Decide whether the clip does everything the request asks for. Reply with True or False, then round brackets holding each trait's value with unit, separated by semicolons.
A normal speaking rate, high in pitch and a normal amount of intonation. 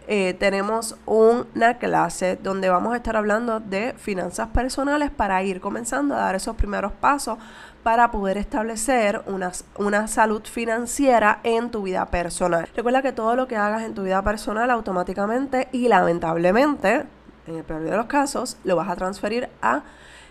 True (160 wpm; 220 Hz; 3.8 semitones)